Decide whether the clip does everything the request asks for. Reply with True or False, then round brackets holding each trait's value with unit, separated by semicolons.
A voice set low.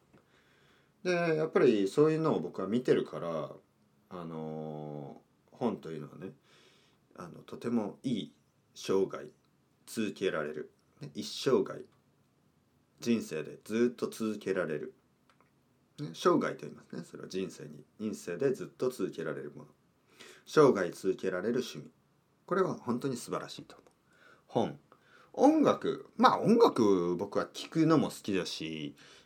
True (105 Hz)